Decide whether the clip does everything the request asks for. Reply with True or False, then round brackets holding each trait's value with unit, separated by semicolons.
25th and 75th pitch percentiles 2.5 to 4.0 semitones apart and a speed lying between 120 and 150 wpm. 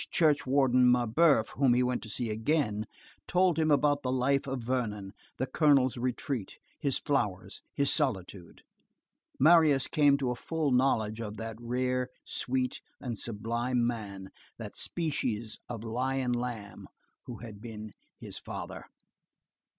True (3.7 semitones; 140 wpm)